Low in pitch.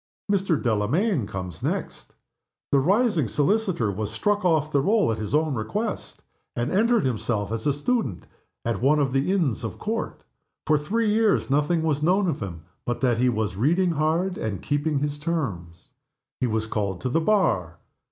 No: medium, 145 Hz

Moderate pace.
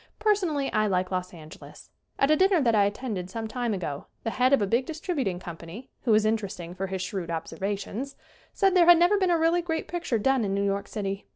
No: fast, 230 wpm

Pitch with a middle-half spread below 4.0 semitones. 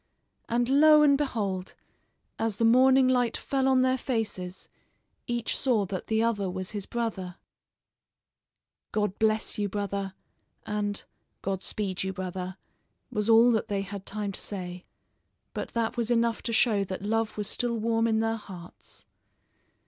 Yes: average, 3.1 semitones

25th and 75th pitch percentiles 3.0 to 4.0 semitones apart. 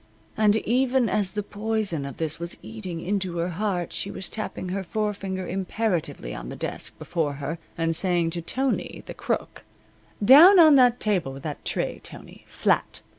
No: average, 4.5 semitones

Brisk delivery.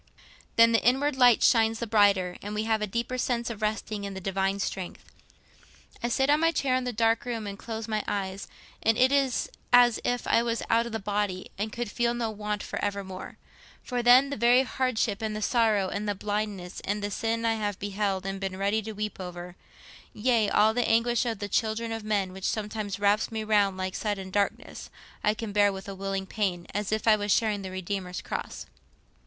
Yes: fast, 210 wpm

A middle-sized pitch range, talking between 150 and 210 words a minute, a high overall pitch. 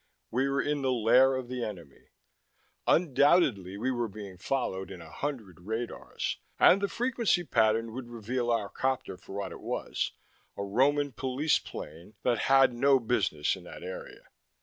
No: average, 5.0 semitones; average, 165 wpm; low, 120 Hz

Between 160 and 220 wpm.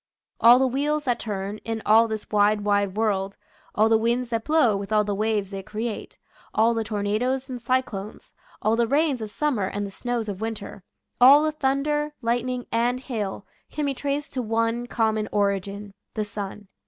Yes: average, 190 wpm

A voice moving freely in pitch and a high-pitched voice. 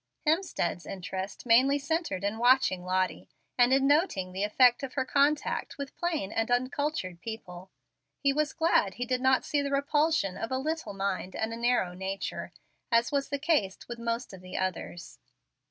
Yes: wide, 6.7 semitones; high, 245 Hz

